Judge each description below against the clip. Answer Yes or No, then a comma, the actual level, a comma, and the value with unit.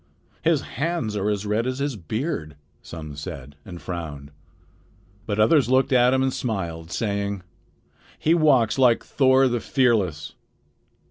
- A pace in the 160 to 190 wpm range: No, average, 140 wpm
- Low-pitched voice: Yes, low, 110 Hz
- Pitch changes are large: Yes, wide, 7.1 semitones